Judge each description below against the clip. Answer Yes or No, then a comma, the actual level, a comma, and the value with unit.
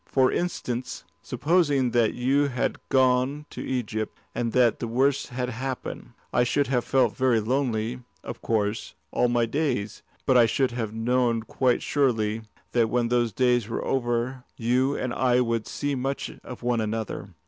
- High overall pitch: No, low, 125 Hz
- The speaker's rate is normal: Yes, average, 165 wpm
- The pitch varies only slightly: Yes, narrow, 2.3 semitones